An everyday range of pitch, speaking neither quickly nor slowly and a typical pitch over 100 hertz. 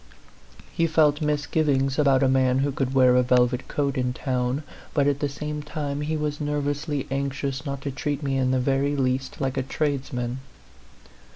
No: narrow, 2.0 semitones; average, 185 wpm; medium, 140 Hz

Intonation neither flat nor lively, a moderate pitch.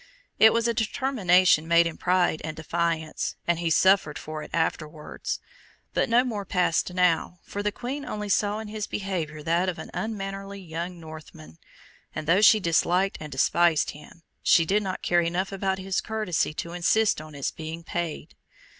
Yes: average, 3.7 semitones; medium, 180 Hz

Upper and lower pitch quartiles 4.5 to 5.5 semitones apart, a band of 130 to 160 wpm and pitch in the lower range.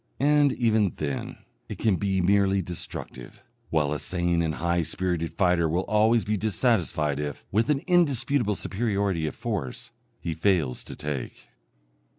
Yes: average, 5.1 semitones; average, 150 wpm; very low, 95 Hz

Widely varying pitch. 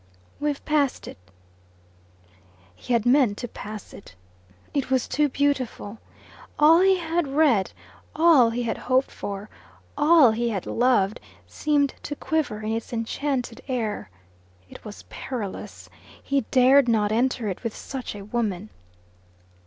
No: average, 4.7 semitones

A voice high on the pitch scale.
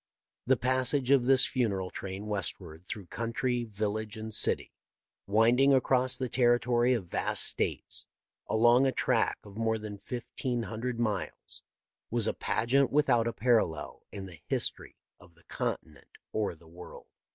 No: low, 115 Hz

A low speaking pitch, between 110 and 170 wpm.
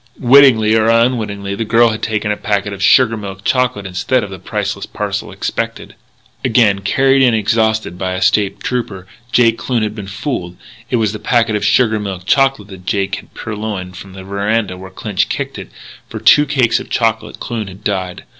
No: low, 105 Hz; average, 195 wpm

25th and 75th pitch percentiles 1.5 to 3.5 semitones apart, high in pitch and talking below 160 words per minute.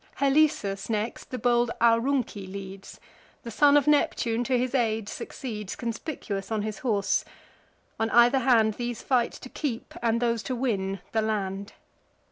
Yes: average, 3.2 semitones; high, 230 Hz; average, 150 wpm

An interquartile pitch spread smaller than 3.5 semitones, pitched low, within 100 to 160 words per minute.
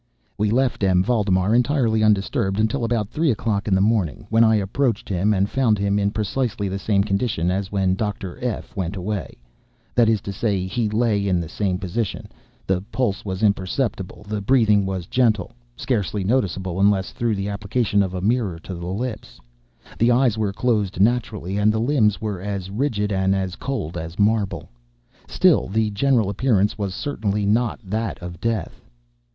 No: average, 3.0 semitones; low, 105 Hz; average, 175 wpm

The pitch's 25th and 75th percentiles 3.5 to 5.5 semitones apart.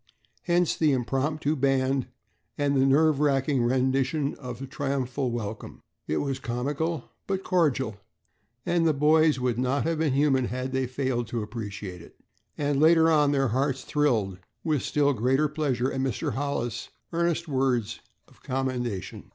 No: average, 3.1 semitones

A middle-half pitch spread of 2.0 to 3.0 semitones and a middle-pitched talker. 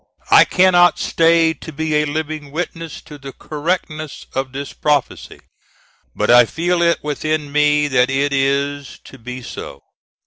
Yes: narrow, 2.6 semitones; medium, 150 Hz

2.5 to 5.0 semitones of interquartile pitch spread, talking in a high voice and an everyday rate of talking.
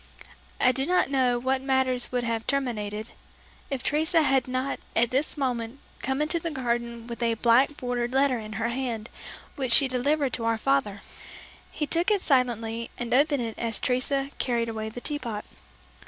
Yes: average, 2.9 semitones; very high, 250 Hz; average, 180 wpm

